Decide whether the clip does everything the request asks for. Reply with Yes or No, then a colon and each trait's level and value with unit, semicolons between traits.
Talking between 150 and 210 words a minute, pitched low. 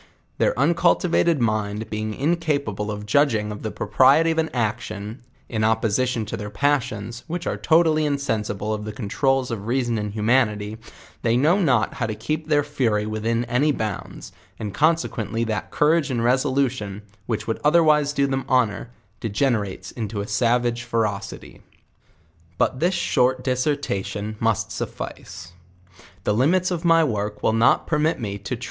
Yes: average, 165 wpm; low, 120 Hz